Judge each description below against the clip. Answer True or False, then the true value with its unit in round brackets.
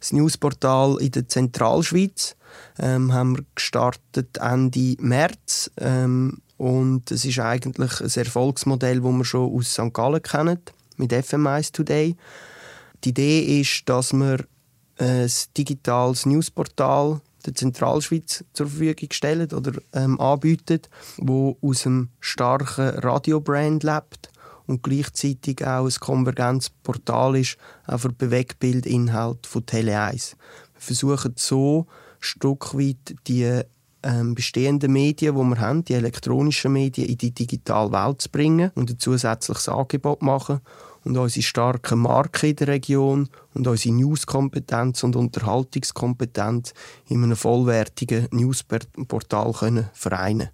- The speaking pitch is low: True (130 Hz)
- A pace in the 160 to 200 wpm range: False (125 wpm)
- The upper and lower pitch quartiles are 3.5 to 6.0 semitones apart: False (2.5 semitones)